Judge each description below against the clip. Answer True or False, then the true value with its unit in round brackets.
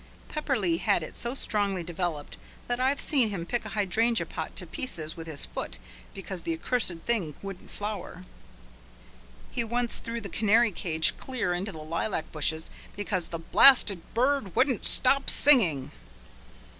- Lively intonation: True (6.1 semitones)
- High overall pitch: True (200 Hz)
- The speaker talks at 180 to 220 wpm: False (155 wpm)